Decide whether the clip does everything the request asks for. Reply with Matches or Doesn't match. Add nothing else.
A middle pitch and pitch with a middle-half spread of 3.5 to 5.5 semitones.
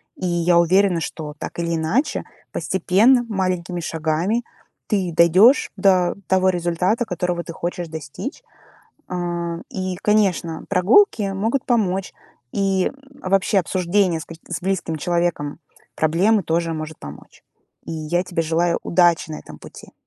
Doesn't match